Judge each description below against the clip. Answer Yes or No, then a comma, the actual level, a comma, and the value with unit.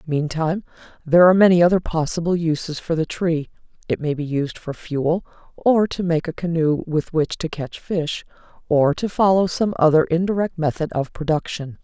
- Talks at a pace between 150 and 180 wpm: Yes, average, 175 wpm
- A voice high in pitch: No, medium, 165 Hz